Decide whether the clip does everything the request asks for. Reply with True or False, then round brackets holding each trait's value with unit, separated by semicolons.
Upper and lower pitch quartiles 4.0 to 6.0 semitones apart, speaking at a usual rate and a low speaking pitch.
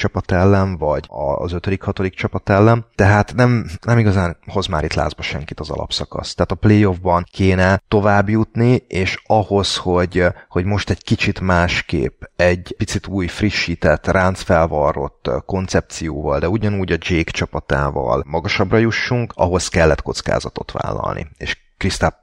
False (2.9 semitones; 140 wpm; 95 Hz)